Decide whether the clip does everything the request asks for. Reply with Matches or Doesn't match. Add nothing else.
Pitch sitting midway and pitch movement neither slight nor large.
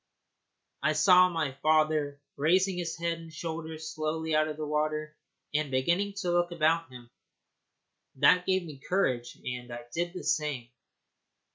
Doesn't match